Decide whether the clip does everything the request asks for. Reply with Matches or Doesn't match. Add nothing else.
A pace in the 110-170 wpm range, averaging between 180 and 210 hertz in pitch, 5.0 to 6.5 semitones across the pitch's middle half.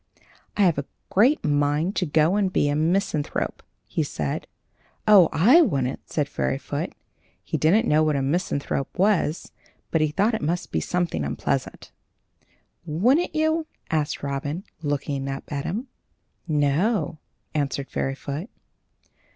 Doesn't match